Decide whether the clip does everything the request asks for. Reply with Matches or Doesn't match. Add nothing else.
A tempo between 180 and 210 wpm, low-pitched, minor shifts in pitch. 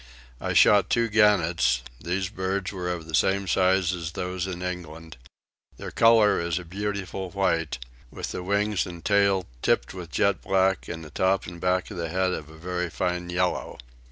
Matches